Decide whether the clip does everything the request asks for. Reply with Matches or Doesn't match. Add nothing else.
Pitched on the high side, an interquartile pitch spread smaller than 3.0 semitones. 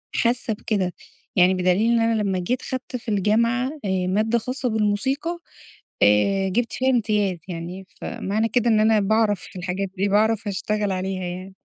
Doesn't match